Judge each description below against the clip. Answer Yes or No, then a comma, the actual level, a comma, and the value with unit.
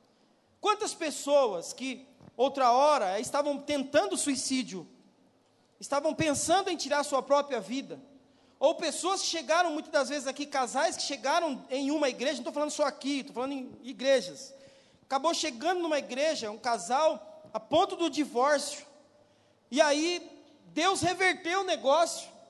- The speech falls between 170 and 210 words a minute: No, average, 145 wpm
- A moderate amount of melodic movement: Yes, average, 3.0 semitones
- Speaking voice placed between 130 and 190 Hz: No, very high, 290 Hz